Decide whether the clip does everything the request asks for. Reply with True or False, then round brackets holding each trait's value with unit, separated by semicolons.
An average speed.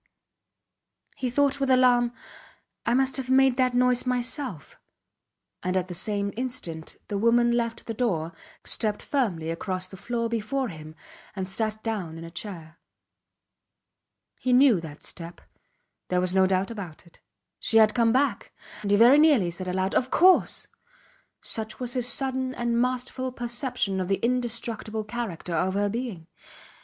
True (155 wpm)